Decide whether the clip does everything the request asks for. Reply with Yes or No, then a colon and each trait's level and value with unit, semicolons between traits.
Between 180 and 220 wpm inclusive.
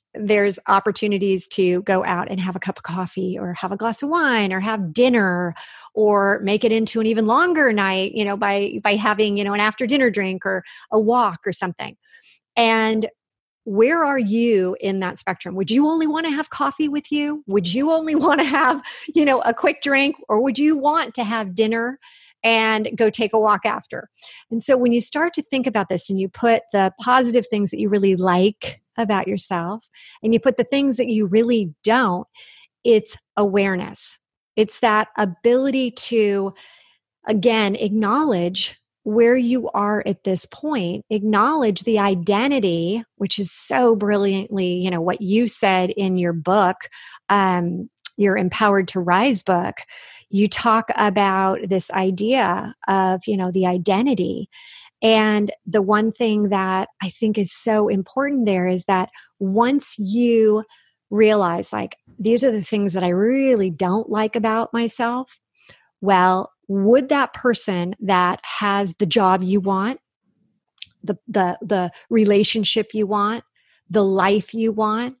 No: average, 165 wpm